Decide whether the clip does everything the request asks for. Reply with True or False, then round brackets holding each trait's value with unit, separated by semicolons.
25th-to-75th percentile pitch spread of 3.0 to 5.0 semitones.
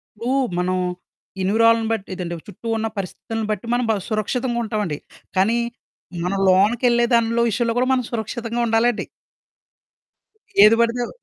False (2.5 semitones)